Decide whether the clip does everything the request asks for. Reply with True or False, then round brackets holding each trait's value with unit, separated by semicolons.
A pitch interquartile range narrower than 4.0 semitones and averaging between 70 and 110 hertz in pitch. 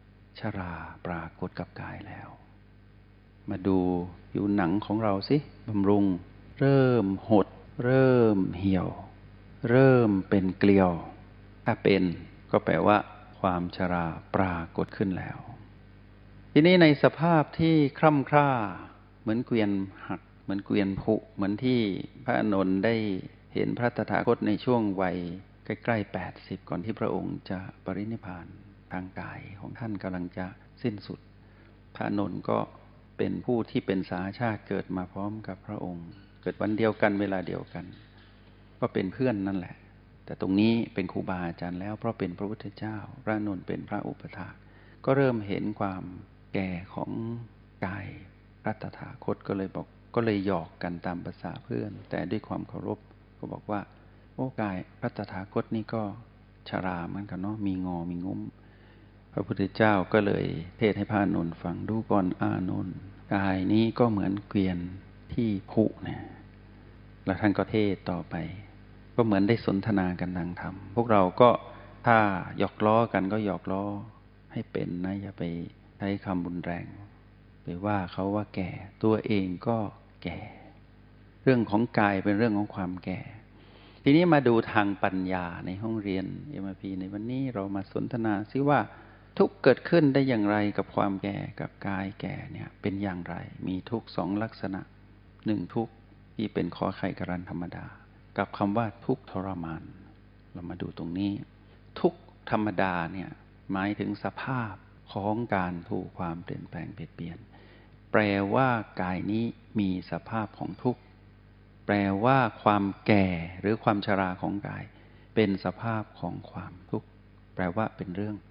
True (2.4 semitones; 100 Hz)